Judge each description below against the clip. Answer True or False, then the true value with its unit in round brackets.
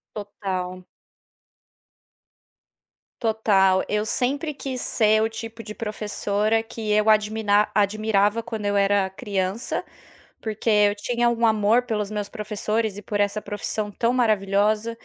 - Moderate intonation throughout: False (1.7 semitones)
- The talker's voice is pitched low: False (215 Hz)